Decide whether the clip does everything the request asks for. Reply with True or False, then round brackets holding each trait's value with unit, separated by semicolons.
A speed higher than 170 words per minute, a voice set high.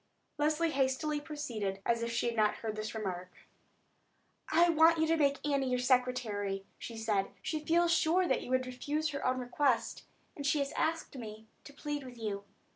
True (190 wpm; 260 Hz)